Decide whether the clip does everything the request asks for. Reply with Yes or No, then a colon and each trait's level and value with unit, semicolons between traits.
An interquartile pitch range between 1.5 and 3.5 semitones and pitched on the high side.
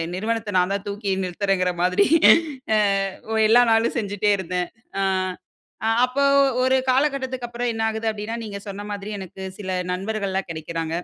Yes: average, 3.1 semitones; high, 205 Hz